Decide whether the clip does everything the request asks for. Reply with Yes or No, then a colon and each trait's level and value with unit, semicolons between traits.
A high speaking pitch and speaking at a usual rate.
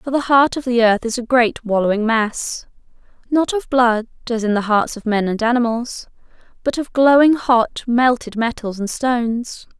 Yes: high, 240 Hz; average, 185 wpm